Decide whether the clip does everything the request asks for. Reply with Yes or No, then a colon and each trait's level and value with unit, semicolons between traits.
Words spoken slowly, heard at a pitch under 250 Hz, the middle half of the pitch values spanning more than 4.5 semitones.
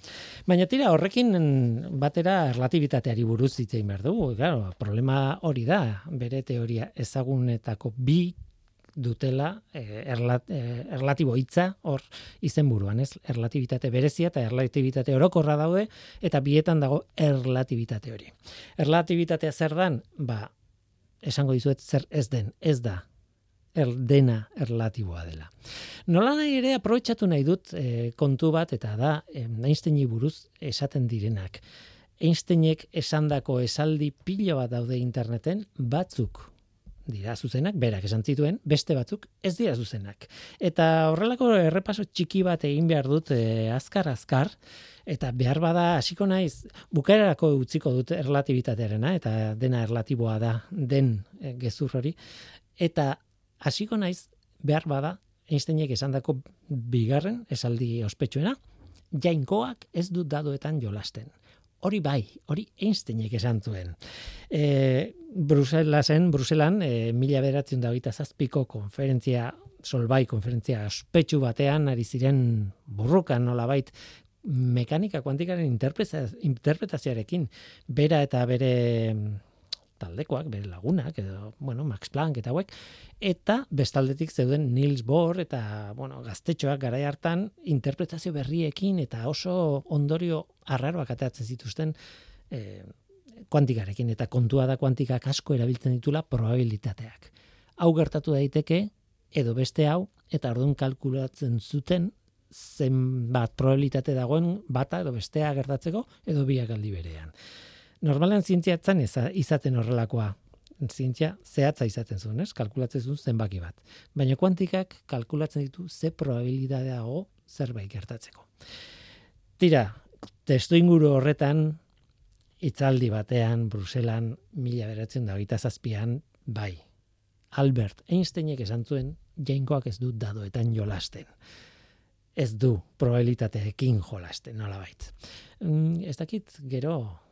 Yes: slow, 115 wpm; low, 135 Hz; average, 5.0 semitones